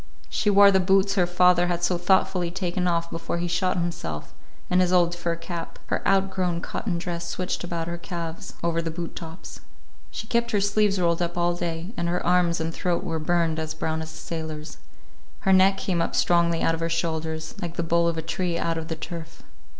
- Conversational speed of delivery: No, fast, 215 wpm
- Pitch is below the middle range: No, medium, 170 Hz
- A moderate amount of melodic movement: No, narrow, 1.6 semitones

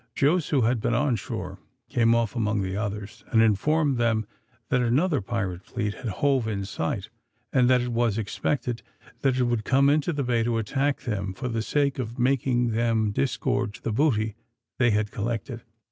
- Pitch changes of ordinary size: Yes, average, 3.4 semitones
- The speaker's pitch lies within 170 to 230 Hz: No, low, 120 Hz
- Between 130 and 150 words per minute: No, average, 185 wpm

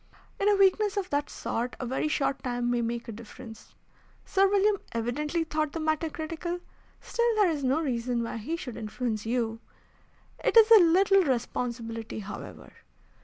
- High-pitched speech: Yes, very high, 280 Hz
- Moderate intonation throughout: No, wide, 7.0 semitones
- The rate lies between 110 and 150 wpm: No, average, 170 wpm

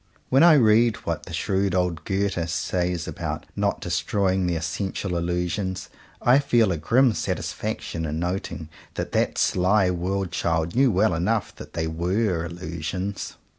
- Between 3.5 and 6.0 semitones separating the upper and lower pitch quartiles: No, average, 3.1 semitones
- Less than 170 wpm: Yes, average, 150 wpm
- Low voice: Yes, very low, 90 Hz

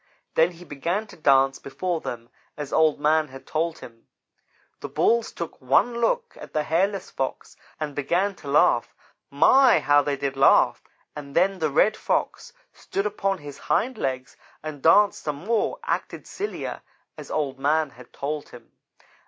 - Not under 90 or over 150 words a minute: No, average, 165 wpm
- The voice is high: No, medium, 155 Hz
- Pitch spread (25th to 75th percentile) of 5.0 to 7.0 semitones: Yes, wide, 5.6 semitones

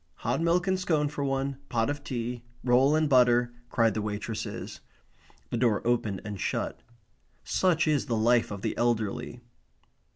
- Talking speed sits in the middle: Yes, average, 160 wpm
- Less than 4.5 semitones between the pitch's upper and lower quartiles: Yes, average, 4.1 semitones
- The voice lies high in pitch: No, low, 120 Hz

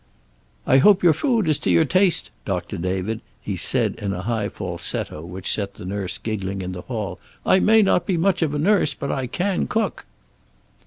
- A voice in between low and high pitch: No, low, 120 Hz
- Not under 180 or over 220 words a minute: Yes, average, 200 wpm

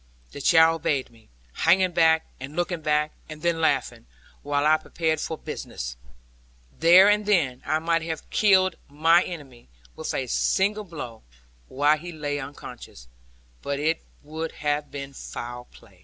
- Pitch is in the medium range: Yes, medium, 155 Hz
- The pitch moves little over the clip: No, average, 3.0 semitones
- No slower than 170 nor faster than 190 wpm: No, average, 155 wpm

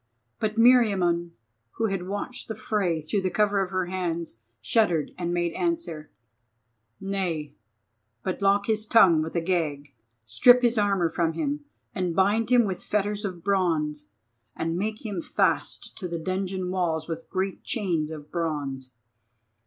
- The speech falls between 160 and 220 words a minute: No, average, 150 wpm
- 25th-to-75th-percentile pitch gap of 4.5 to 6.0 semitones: No, average, 3.9 semitones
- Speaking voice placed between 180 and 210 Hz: Yes, medium, 185 Hz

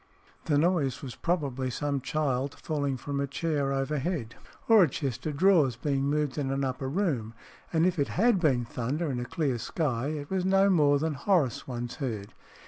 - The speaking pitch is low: No, medium, 145 Hz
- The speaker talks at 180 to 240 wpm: Yes, average, 190 wpm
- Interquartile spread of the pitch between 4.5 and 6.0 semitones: No, average, 3.6 semitones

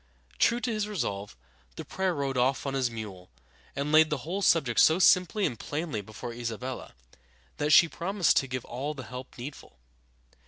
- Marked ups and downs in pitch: Yes, wide, 5.7 semitones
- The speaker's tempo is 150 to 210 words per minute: Yes, average, 180 wpm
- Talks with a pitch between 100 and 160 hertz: Yes, low, 135 Hz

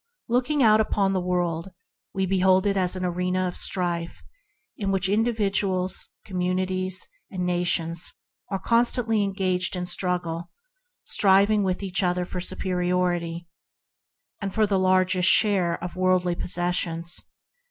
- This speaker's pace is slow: Yes, slow, 130 wpm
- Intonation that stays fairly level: Yes, narrow, 1.6 semitones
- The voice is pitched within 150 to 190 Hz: Yes, medium, 185 Hz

